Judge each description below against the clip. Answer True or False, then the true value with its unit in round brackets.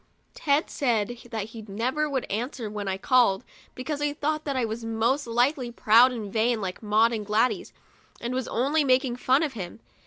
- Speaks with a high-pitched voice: True (240 Hz)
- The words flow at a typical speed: True (190 wpm)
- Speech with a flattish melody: False (3.3 semitones)